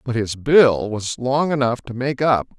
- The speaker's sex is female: No, male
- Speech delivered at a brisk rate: Yes, fast, 210 wpm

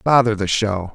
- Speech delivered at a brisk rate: No, average, 190 wpm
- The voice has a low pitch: Yes, low, 105 Hz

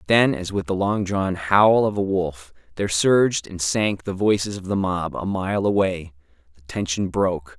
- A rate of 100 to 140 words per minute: No, average, 200 wpm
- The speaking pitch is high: No, very low, 95 Hz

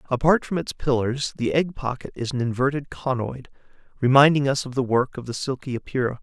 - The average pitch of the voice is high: No, low, 130 Hz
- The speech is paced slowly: No, average, 195 wpm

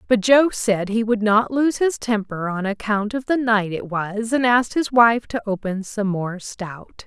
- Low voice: No, high, 220 Hz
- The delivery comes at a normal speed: No, fast, 210 wpm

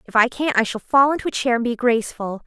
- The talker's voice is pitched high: Yes, high, 240 Hz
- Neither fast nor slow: No, fast, 290 wpm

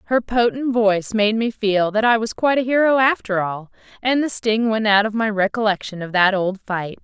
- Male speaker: No, female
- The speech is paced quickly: Yes, fast, 220 wpm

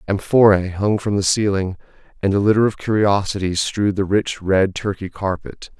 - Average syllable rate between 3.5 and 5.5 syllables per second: Yes, 5.1 syllables/s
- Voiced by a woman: No, male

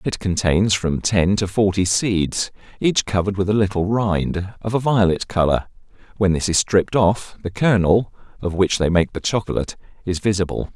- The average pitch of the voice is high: No, very low, 95 Hz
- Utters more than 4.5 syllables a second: Yes, 5.0 syllables/s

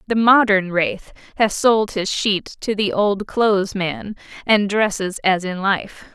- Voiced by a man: No, female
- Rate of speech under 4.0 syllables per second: Yes, 3.6 syllables/s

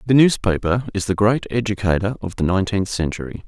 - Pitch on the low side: Yes, low, 100 Hz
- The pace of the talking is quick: No, average, 175 wpm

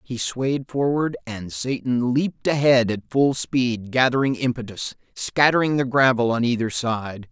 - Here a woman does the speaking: No, male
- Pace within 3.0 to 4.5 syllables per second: Yes, 4.4 syllables/s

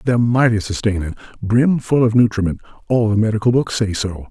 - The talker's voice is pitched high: No, low, 110 Hz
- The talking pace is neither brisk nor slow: Yes, average, 155 wpm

